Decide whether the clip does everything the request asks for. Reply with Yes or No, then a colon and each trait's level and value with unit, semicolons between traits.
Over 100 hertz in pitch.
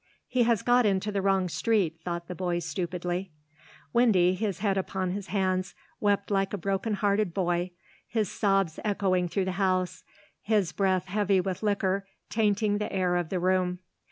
Yes: high, 190 Hz